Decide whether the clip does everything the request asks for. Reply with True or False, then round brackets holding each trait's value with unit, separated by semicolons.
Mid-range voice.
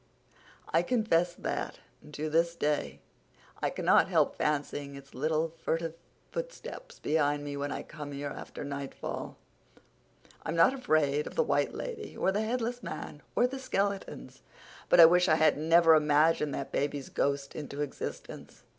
True (155 Hz)